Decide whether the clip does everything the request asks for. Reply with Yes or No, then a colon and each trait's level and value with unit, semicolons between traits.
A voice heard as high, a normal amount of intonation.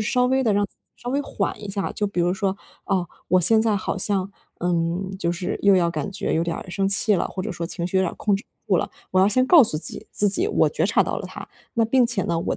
Yes: high, 195 Hz; average, 3.6 semitones